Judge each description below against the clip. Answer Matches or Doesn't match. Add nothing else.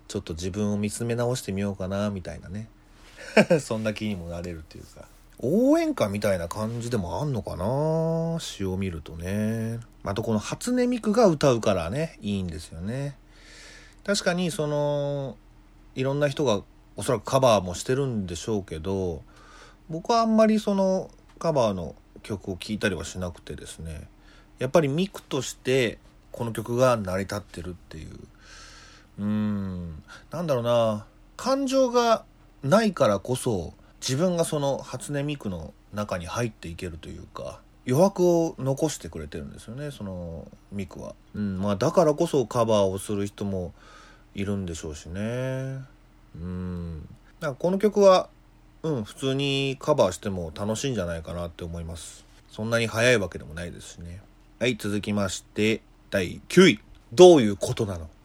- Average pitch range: Doesn't match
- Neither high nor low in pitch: Doesn't match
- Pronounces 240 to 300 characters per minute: Doesn't match